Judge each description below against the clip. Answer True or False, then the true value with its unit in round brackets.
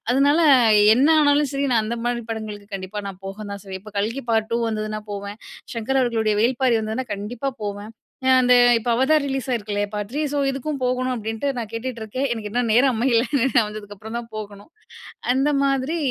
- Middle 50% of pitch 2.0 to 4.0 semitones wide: True (3.6 semitones)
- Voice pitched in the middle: False (230 Hz)